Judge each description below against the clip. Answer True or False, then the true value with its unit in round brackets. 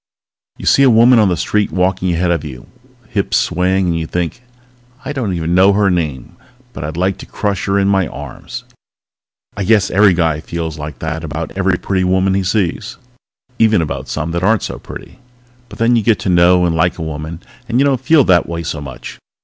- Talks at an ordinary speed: False (215 wpm)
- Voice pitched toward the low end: True (90 Hz)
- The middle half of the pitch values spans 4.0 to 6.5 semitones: False (3.5 semitones)